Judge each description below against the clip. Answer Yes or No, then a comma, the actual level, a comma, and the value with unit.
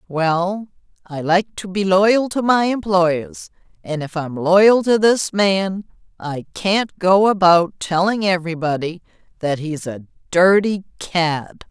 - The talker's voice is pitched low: No, medium, 185 Hz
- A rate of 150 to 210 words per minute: No, average, 140 wpm